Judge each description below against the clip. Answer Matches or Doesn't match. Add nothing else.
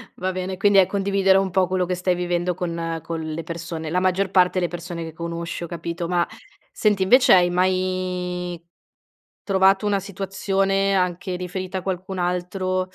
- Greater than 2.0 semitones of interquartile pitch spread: Doesn't match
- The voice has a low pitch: Doesn't match